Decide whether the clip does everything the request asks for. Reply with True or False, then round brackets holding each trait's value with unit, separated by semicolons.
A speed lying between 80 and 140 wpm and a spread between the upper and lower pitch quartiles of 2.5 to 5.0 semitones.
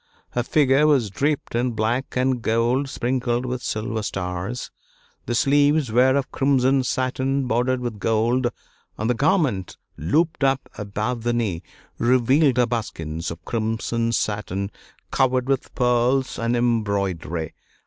True (135 wpm; 3.1 semitones)